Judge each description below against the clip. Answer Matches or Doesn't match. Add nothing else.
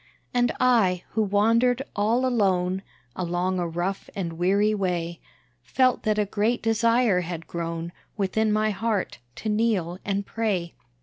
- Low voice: Doesn't match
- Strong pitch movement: Doesn't match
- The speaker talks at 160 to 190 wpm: Doesn't match